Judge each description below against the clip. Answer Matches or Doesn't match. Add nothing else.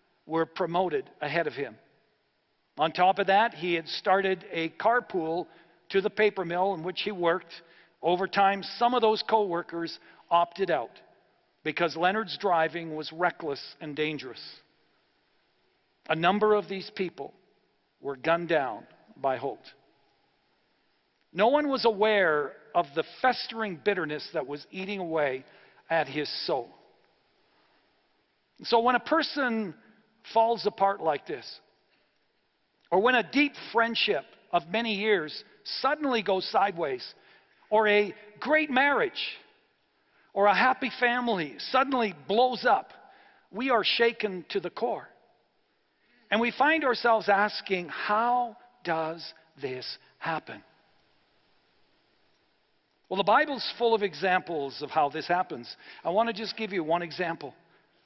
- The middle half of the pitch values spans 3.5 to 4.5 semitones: Doesn't match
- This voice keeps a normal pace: Doesn't match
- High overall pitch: Matches